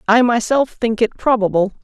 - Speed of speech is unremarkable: Yes, average, 165 wpm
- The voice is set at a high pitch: Yes, high, 230 Hz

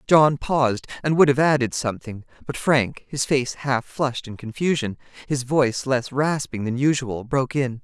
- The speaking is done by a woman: Yes, female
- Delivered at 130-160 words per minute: No, average, 175 wpm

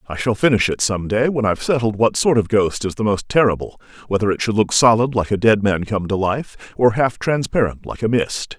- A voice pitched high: No, low, 110 Hz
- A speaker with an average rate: No, fast, 240 wpm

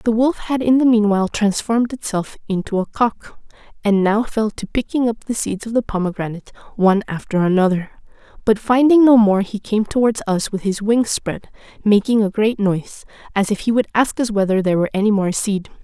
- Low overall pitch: No, high, 215 Hz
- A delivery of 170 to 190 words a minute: No, average, 200 wpm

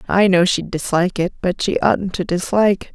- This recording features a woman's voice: Yes, female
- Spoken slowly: No, fast, 205 wpm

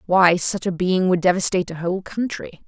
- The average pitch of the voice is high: No, medium, 180 Hz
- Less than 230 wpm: Yes, average, 200 wpm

